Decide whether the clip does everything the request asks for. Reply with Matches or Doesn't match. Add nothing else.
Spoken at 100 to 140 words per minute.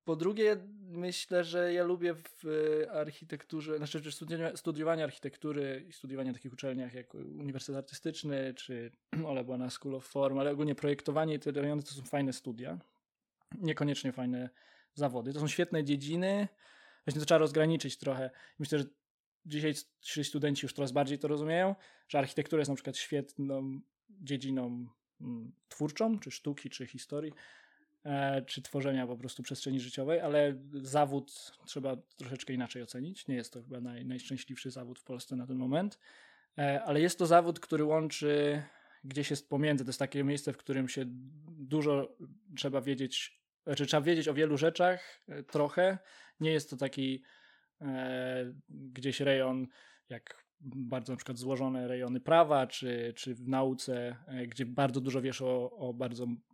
Doesn't match